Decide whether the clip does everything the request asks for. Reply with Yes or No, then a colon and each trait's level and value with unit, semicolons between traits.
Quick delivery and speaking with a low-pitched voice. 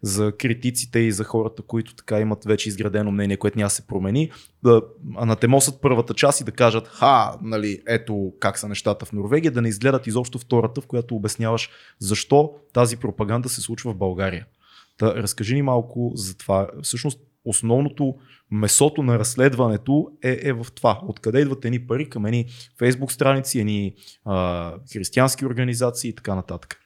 Yes: fast, 170 wpm; low, 115 Hz